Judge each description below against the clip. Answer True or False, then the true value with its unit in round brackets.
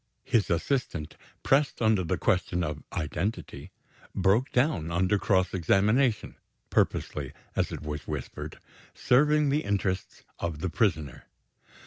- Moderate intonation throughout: False (6.1 semitones)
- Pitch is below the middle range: True (95 Hz)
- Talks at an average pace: False (120 wpm)